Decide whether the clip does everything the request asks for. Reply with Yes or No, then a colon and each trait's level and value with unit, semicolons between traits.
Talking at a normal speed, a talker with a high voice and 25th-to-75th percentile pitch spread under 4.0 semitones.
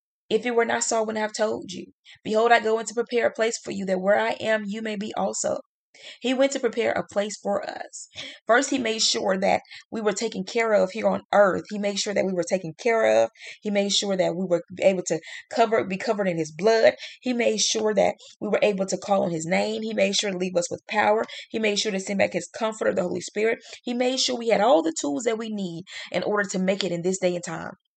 No: fast, 265 wpm; high, 210 Hz; average, 3.0 semitones